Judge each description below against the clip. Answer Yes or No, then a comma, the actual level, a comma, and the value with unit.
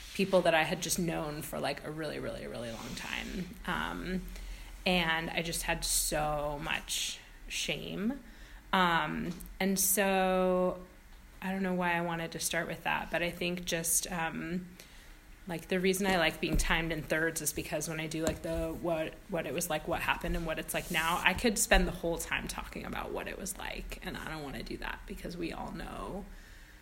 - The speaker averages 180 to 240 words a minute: Yes, fast, 205 wpm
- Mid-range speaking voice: Yes, medium, 170 Hz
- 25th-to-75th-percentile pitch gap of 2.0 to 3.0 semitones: Yes, narrow, 2.4 semitones